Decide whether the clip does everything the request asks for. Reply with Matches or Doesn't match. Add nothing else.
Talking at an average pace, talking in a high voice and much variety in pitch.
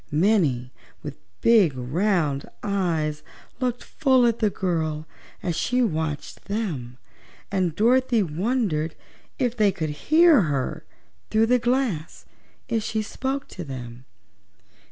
Doesn't match